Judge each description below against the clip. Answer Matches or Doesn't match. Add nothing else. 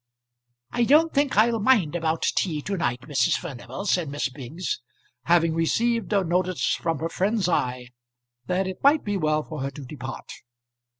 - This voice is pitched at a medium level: Matches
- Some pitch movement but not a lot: Doesn't match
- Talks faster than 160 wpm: Matches